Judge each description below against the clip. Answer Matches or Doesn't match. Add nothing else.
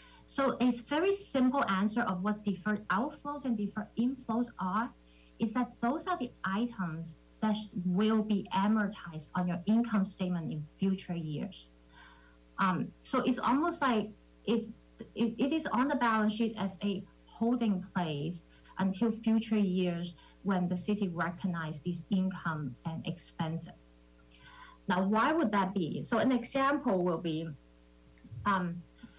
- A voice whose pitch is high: Matches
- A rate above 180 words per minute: Doesn't match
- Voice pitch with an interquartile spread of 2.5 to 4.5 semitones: Doesn't match